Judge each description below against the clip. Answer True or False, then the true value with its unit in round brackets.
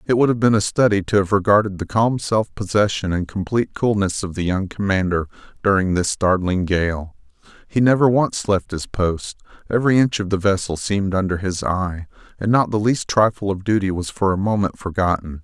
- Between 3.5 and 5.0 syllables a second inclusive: False (5.4 syllables/s)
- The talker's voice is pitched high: False (100 Hz)